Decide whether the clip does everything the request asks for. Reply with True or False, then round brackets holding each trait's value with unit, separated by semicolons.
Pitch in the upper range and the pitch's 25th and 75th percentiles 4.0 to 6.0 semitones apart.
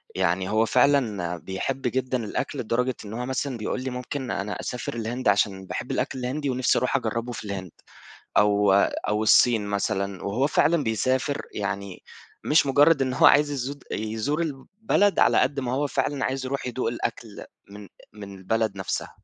False (120 Hz; 4.6 semitones)